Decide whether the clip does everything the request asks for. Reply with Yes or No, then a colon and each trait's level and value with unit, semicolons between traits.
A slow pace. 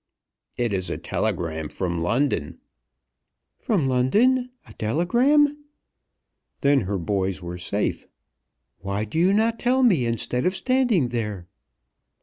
Yes: slow, 125 wpm